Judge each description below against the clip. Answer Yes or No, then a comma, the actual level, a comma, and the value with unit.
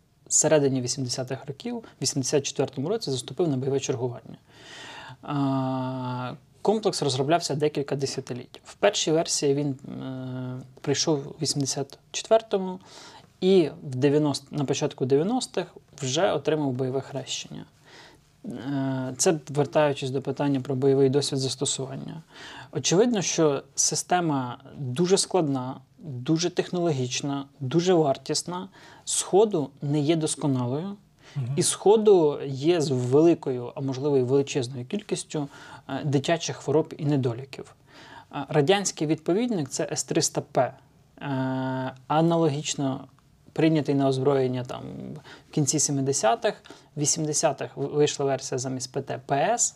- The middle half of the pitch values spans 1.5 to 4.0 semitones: Yes, average, 2.8 semitones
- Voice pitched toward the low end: No, medium, 145 Hz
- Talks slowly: Yes, slow, 100 wpm